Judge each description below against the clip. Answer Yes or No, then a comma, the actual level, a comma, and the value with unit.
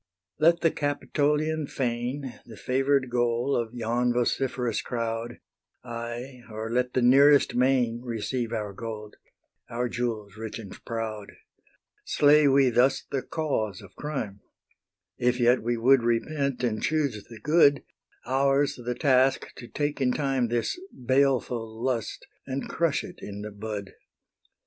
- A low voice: Yes, low, 125 Hz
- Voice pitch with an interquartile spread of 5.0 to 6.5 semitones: No, average, 3.1 semitones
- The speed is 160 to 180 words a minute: No, average, 140 wpm